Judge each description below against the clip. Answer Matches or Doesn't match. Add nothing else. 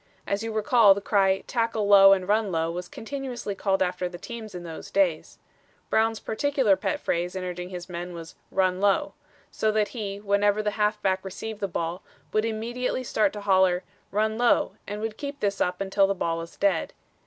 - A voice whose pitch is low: Doesn't match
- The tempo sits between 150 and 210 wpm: Matches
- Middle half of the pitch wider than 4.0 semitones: Doesn't match